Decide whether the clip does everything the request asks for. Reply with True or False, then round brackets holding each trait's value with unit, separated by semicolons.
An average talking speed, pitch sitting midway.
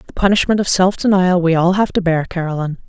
False (230 wpm; 180 Hz)